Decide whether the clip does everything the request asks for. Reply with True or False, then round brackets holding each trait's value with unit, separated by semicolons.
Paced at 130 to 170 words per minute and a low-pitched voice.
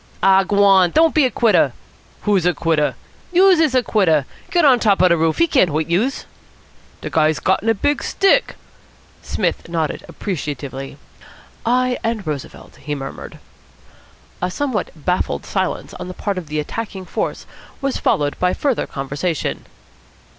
False (155 wpm; 190 Hz)